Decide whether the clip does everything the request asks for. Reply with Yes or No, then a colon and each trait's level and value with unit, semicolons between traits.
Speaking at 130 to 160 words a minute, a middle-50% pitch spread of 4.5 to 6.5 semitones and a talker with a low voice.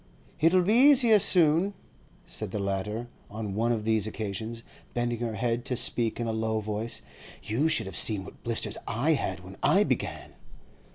No: average, 175 wpm; average, 5.0 semitones; low, 115 Hz